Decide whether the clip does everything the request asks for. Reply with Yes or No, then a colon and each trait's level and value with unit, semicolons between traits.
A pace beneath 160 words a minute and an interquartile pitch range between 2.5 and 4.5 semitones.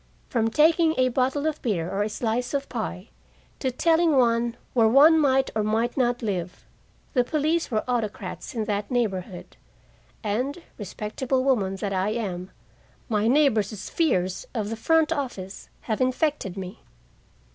No: average, 150 wpm; average, 4.9 semitones